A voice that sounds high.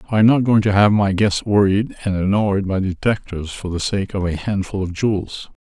No: low, 100 Hz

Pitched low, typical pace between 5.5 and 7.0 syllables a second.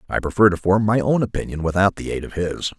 Yes: very low, 95 Hz; 6.4 syllables/s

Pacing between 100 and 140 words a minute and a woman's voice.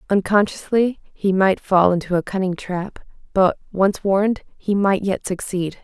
Yes: slow, 135 wpm; female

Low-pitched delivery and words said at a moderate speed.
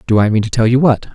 No: low, 115 Hz; fast, 365 wpm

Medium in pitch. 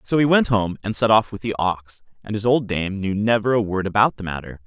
No: low, 105 Hz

